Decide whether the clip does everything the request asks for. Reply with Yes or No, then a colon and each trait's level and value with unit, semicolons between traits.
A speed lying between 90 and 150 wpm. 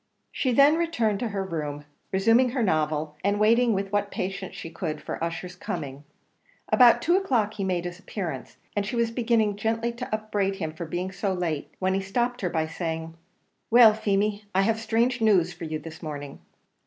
No: average, 190 wpm